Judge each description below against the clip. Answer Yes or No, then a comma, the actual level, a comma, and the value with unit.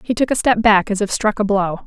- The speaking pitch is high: Yes, high, 210 Hz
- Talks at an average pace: No, fast, 320 wpm